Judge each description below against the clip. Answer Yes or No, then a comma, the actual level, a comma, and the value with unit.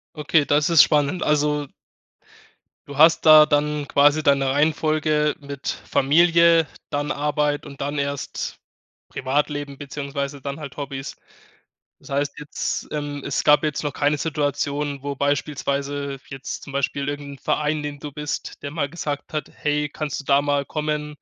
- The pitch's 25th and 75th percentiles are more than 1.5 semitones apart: No, narrow, 1.1 semitones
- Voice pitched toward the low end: No, medium, 145 Hz